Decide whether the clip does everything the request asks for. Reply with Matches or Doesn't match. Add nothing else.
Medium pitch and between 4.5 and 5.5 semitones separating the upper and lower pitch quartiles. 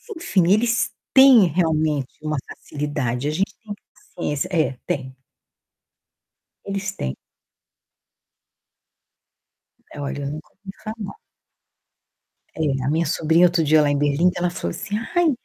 Matches